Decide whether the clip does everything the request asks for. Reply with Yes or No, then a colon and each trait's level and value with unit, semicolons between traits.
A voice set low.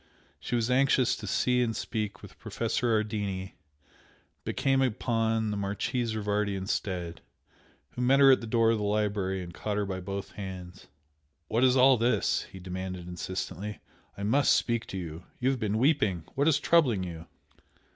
Yes: low, 105 Hz